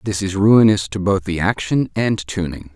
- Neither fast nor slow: Yes, average, 195 wpm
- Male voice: Yes, male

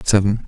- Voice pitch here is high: No, low, 100 Hz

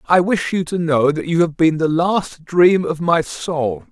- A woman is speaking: No, male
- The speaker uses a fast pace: Yes, fast, 230 wpm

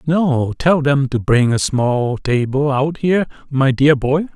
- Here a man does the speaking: Yes, male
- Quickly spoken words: No, average, 180 wpm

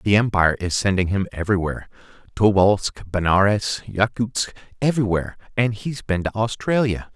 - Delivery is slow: Yes, slow, 115 wpm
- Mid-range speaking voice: No, low, 105 Hz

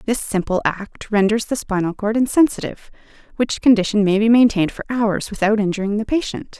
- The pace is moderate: Yes, average, 175 wpm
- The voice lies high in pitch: Yes, high, 215 Hz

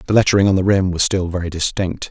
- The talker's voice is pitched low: Yes, very low, 95 Hz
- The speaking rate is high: Yes, fast, 255 wpm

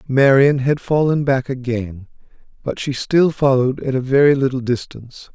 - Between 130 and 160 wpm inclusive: Yes, average, 155 wpm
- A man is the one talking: Yes, male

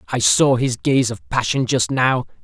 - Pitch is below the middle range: Yes, low, 120 Hz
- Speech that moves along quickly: No, average, 195 wpm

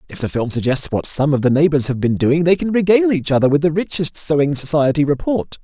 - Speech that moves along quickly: Yes, fast, 245 wpm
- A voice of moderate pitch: Yes, medium, 150 Hz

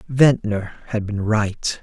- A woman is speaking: No, male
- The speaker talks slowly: Yes, slow, 130 wpm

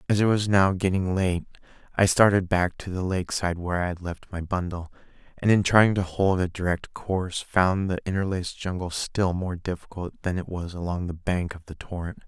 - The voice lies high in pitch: No, very low, 90 Hz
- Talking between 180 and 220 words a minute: Yes, fast, 205 wpm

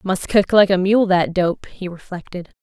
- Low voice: No, medium, 185 Hz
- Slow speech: No, fast, 205 wpm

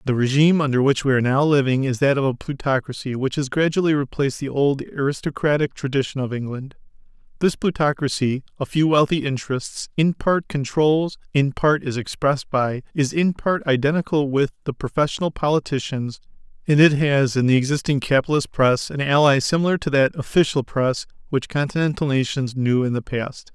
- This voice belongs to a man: Yes, male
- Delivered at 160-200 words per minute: Yes, average, 165 wpm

